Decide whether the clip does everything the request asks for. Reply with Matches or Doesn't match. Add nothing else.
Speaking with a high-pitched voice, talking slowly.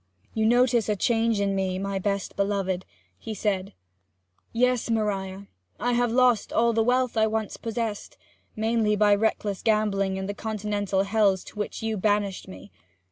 Doesn't match